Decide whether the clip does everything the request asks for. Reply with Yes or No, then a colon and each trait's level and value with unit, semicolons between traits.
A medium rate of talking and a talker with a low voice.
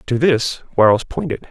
Yes: average, 160 wpm; low, 120 Hz